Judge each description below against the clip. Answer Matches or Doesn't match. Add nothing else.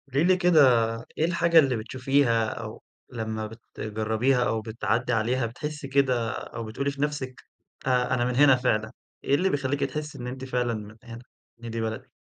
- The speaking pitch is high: Doesn't match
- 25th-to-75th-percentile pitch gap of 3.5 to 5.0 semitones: Matches